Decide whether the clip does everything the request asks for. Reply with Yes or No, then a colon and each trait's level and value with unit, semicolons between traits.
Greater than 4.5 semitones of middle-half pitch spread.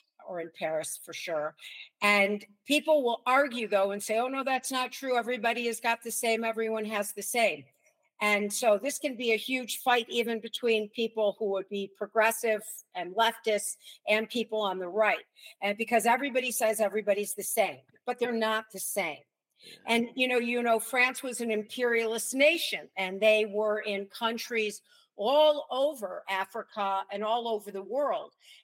No: average, 3.1 semitones